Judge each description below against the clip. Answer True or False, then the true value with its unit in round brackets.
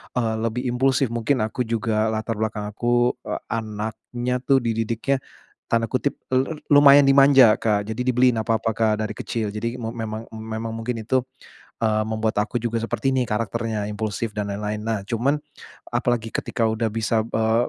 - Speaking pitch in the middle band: False (115 Hz)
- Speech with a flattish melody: True (2.0 semitones)